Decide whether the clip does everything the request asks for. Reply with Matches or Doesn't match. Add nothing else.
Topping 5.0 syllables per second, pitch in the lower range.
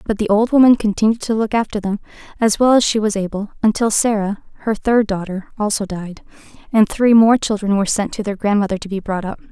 Doesn't match